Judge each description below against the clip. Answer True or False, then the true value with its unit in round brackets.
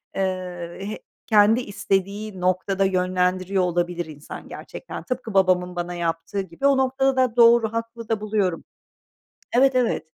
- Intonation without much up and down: False (4.2 semitones)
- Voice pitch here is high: True (195 Hz)